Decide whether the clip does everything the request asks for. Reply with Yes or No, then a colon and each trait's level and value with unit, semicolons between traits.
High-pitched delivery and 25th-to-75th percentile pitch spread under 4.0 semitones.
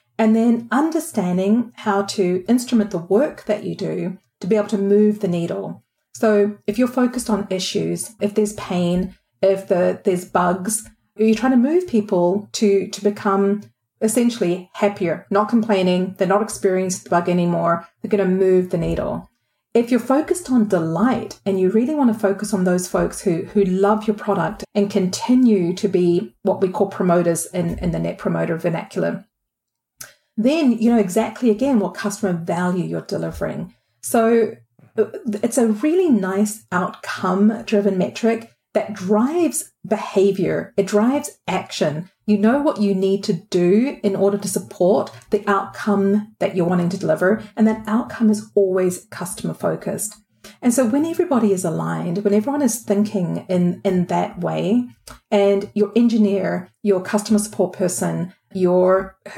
Yes: high, 205 Hz; average, 2.9 semitones